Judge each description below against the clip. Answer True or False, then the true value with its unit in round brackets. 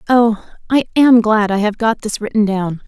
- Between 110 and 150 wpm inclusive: False (210 wpm)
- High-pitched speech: True (220 Hz)